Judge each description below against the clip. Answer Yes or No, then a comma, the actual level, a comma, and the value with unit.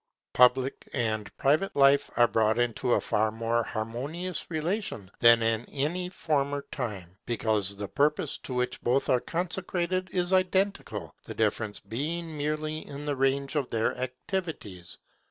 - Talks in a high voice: No, low, 135 Hz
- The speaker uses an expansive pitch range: Yes, wide, 5.8 semitones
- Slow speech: No, average, 145 wpm